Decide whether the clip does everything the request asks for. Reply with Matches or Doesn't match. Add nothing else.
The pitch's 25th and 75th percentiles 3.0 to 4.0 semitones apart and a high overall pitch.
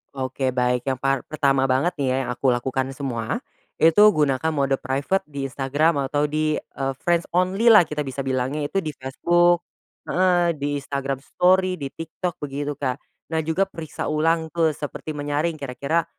Doesn't match